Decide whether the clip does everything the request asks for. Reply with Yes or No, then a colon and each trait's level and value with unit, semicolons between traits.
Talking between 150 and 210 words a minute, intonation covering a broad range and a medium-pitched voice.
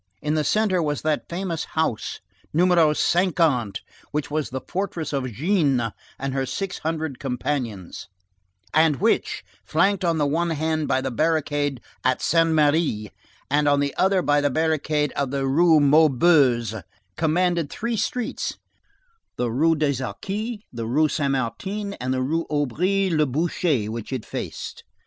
No: average, 155 wpm; average, 4.0 semitones; medium, 150 Hz